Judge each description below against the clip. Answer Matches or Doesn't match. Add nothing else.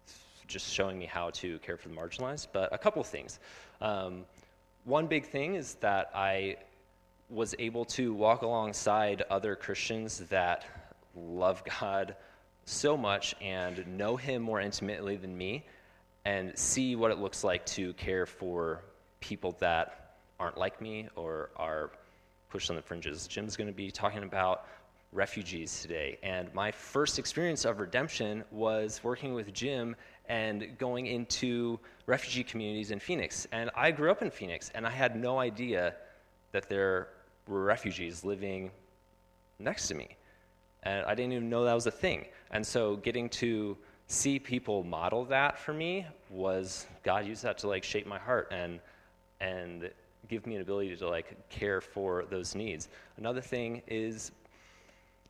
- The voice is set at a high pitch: Doesn't match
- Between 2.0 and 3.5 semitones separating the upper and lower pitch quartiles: Doesn't match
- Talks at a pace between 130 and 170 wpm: Matches